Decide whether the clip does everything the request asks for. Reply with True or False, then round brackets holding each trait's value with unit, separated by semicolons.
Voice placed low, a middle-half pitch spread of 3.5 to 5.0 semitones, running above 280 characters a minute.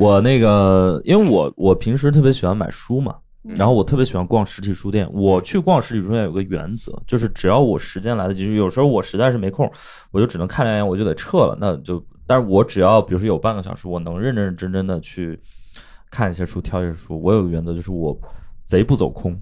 True (100 Hz; 4.0 semitones; 350 characters per minute)